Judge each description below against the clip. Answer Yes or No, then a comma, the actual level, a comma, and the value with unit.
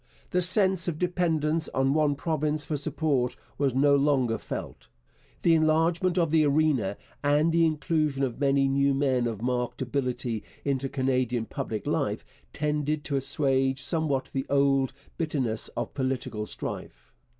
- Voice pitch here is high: No, medium, 140 Hz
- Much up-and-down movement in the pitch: No, average, 3.0 semitones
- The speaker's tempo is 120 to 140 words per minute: No, average, 150 wpm